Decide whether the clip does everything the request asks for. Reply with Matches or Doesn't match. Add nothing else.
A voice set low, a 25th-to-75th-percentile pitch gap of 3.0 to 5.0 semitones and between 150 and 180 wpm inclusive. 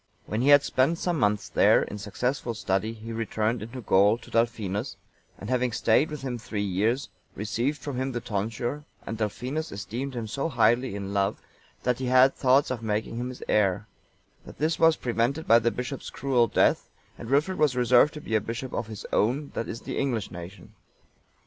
Doesn't match